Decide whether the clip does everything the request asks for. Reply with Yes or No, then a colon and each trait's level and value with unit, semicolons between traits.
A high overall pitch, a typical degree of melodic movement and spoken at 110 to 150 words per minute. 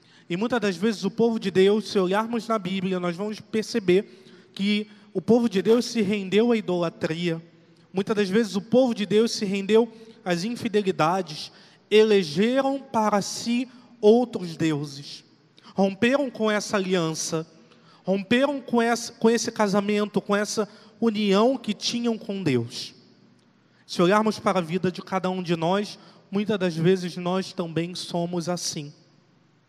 Yes: high, 200 Hz; average, 3.9 semitones; average, 145 wpm